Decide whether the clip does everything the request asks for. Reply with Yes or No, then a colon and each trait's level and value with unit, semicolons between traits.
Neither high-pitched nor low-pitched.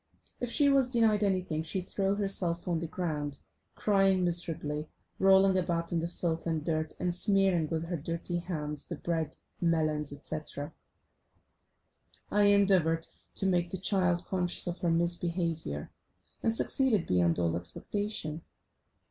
Yes: medium, 175 Hz